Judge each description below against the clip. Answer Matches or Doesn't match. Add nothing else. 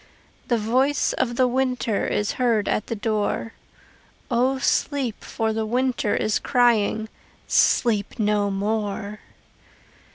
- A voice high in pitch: Matches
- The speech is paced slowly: Matches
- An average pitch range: Matches